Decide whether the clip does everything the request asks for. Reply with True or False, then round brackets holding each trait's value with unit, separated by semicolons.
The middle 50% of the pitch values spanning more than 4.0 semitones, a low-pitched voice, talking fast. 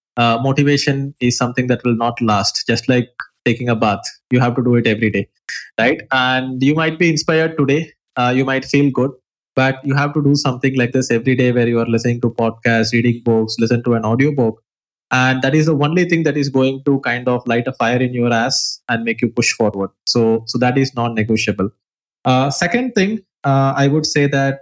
False (2.9 semitones; 125 Hz; 220 wpm)